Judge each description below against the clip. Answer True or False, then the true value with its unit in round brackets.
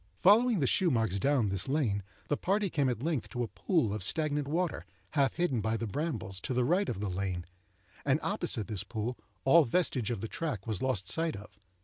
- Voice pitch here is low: True (130 Hz)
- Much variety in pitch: True (7.3 semitones)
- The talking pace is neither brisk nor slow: False (215 wpm)